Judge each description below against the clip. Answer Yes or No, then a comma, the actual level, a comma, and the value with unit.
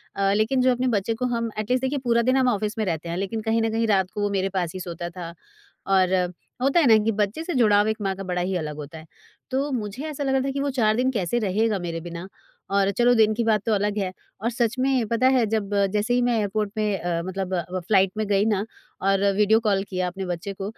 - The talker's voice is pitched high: Yes, high, 210 Hz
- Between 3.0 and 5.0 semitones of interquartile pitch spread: Yes, average, 3.4 semitones